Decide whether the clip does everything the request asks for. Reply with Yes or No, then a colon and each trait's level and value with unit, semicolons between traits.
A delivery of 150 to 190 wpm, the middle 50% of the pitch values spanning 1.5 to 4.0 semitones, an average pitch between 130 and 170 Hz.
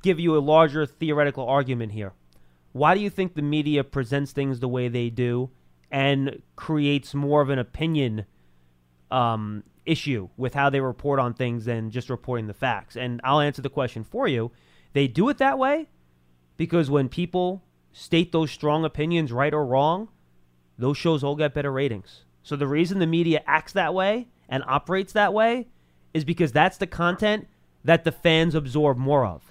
No: average, 180 wpm; average, 4.7 semitones; medium, 140 Hz